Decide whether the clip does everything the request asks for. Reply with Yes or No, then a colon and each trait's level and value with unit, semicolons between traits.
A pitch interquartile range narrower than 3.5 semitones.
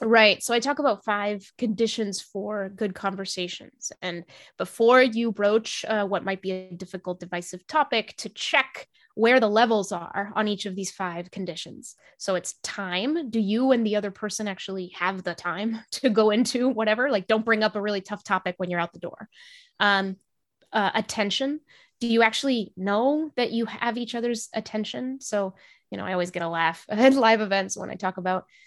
No: average, 3.8 semitones